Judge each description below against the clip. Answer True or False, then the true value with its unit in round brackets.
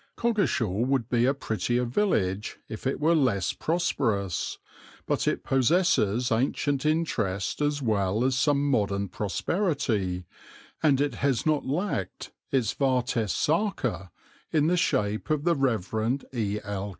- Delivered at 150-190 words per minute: False (135 wpm)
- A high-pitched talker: False (125 Hz)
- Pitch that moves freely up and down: True (6.0 semitones)